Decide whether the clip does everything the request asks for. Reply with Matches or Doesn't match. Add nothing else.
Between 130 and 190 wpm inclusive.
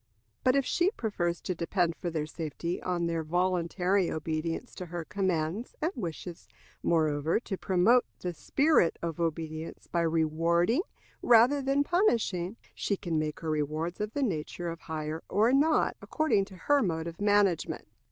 Matches